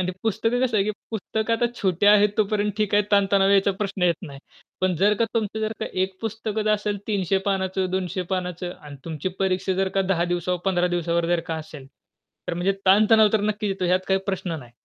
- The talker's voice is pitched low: No, high, 195 Hz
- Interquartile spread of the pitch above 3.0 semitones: No, narrow, 2.6 semitones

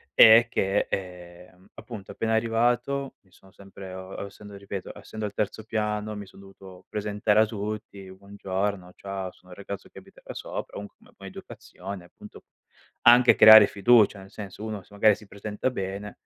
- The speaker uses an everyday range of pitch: No, narrow, 2.0 semitones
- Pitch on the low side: Yes, low, 100 Hz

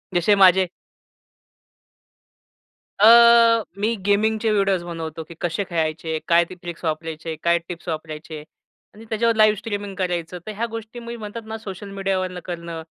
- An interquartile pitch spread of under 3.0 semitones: No, average, 4.2 semitones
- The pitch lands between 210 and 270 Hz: No, medium, 185 Hz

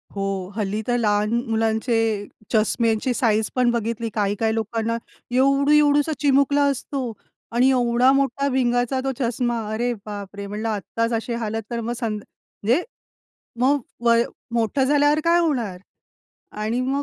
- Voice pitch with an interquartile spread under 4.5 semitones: Yes, average, 3.3 semitones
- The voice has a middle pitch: No, high, 235 Hz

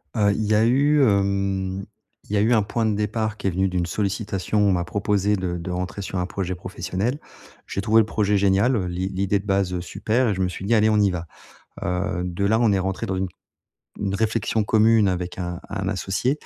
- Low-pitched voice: Yes, low, 100 Hz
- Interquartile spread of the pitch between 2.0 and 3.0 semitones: Yes, narrow, 2.5 semitones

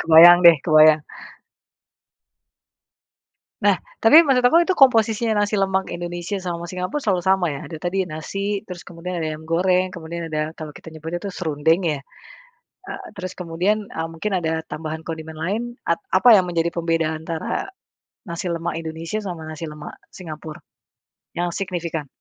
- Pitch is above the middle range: No, medium, 170 Hz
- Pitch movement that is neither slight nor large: Yes, average, 3.0 semitones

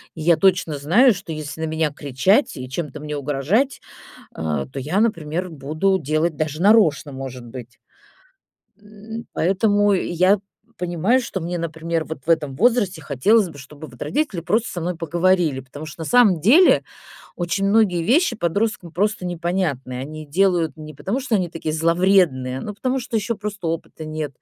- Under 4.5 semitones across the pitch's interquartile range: No, average, 4.8 semitones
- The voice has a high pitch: No, medium, 170 Hz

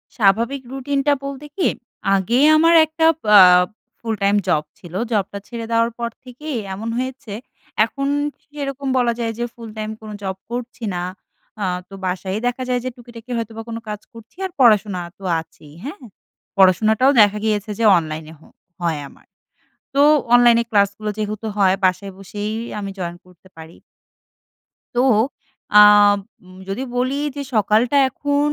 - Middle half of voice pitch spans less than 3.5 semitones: No, average, 4.2 semitones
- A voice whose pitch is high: Yes, high, 220 Hz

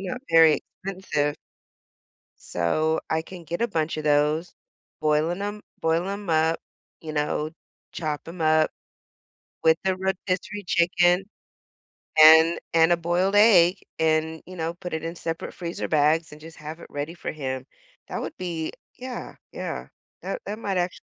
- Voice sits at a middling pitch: Yes, medium, 165 Hz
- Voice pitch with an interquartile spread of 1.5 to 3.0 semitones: Yes, narrow, 2.6 semitones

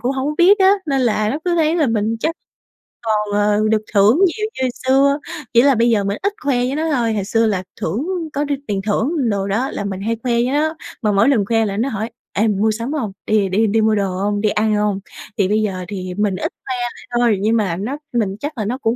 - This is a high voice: Yes, high, 220 Hz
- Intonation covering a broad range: No, average, 4.5 semitones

